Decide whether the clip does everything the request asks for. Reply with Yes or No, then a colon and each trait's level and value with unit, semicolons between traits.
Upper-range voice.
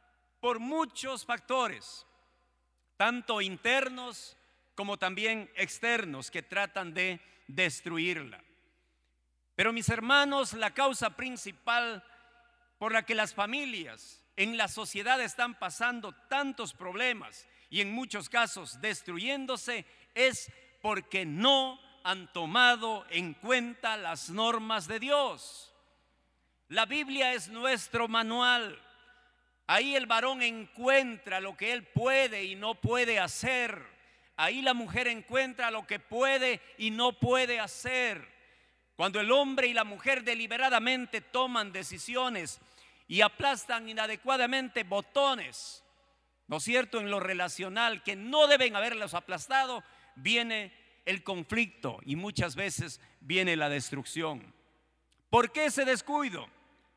Yes: high, 230 Hz